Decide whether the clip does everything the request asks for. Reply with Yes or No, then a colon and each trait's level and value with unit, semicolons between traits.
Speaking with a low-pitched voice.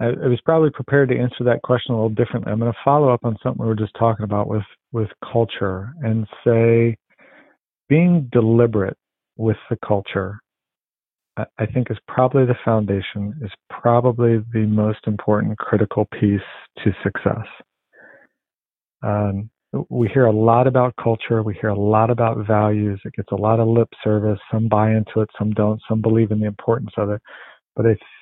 Yes: low, 110 Hz